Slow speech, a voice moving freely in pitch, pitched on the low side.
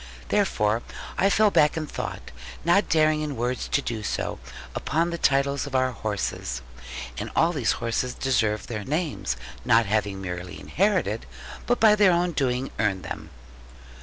No: average, 160 wpm; wide, 7.2 semitones; low, 130 Hz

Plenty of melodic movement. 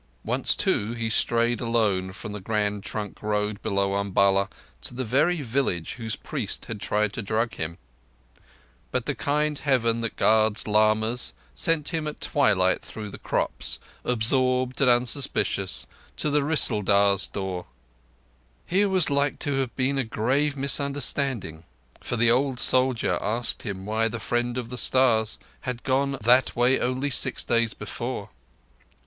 No: average, 4.0 semitones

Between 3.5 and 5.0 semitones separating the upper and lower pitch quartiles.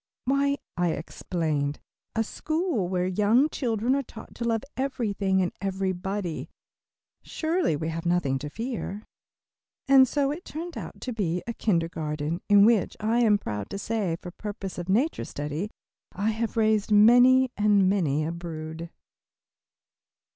No: wide, 5.5 semitones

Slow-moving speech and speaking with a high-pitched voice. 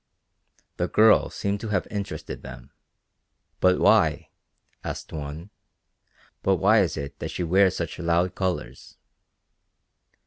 No: slow, 125 wpm; very low, 90 Hz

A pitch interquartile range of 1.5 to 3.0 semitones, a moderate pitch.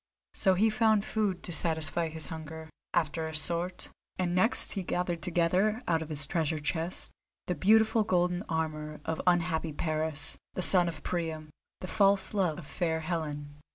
Yes: narrow, 2.5 semitones; medium, 170 Hz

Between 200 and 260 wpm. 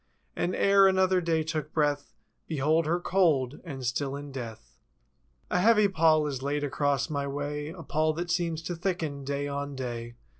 No: average, 175 wpm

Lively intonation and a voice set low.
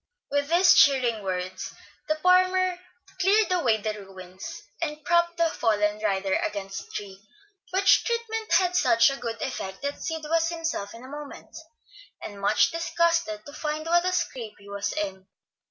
No: wide, 8.7 semitones; very high, 285 Hz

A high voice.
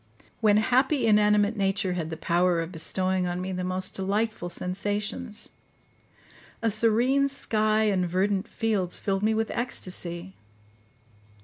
Yes: high, 200 Hz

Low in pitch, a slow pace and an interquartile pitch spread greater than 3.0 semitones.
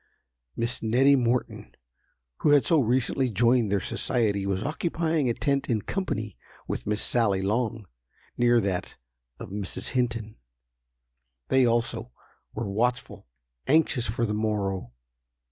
Yes: low, 115 Hz; slow, 125 wpm; average, 3.5 semitones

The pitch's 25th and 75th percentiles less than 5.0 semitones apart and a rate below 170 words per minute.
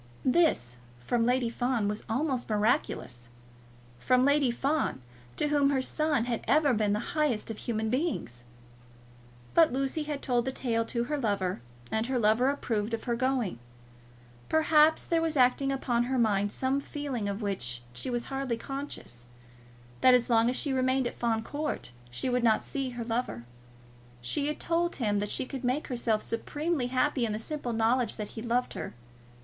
No: average, 3.9 semitones; average, 175 wpm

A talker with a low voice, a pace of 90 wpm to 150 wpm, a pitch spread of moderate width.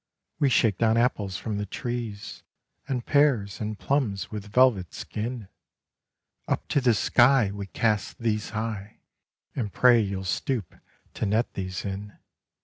Yes: low, 110 Hz; average, 140 wpm; average, 3.3 semitones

